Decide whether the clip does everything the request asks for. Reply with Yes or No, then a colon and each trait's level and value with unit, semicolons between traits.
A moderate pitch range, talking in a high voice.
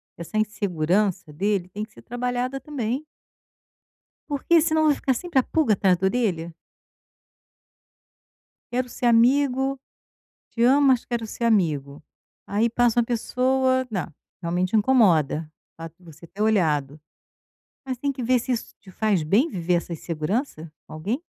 No: wide, 6.6 semitones; high, 220 Hz